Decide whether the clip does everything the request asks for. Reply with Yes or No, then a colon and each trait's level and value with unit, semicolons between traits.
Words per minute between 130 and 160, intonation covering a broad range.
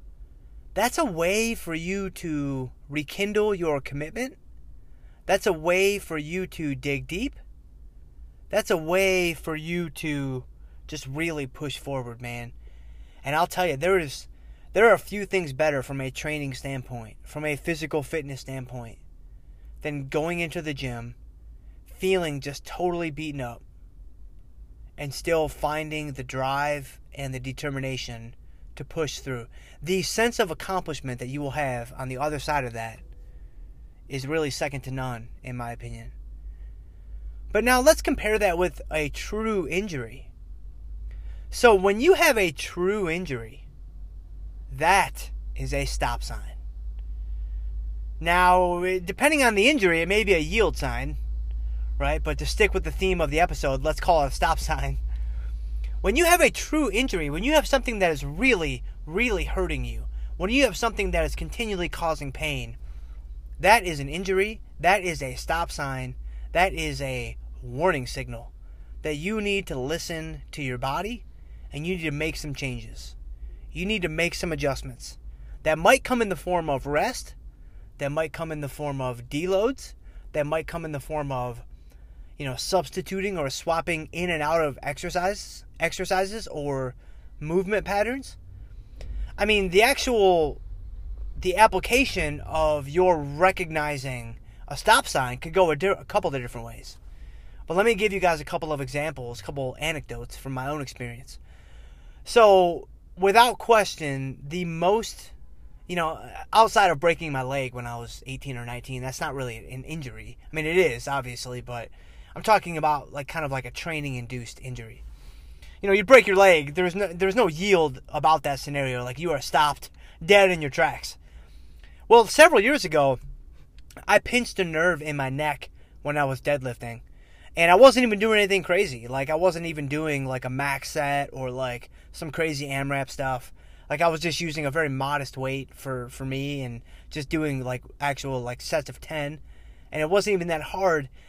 No: average, 170 wpm; wide, 6.4 semitones